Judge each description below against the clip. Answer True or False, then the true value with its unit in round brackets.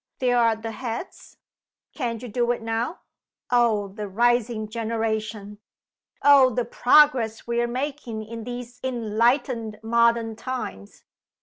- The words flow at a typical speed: False (125 wpm)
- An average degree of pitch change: False (1.9 semitones)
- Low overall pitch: False (235 Hz)